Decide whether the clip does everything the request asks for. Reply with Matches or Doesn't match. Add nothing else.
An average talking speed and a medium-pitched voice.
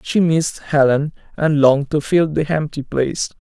Matches